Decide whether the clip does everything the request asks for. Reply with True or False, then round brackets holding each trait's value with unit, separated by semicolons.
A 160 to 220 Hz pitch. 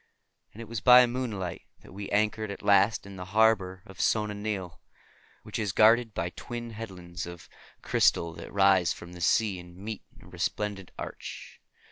False (100 Hz)